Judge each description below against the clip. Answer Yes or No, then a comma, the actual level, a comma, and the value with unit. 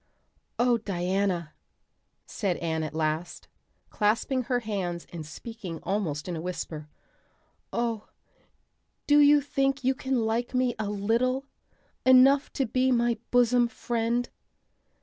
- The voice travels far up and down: Yes, wide, 6.0 semitones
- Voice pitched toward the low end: No, high, 230 Hz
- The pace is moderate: No, slow, 125 wpm